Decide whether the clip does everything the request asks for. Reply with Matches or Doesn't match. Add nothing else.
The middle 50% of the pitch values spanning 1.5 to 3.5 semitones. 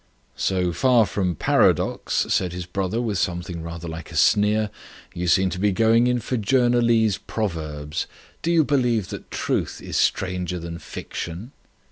Doesn't match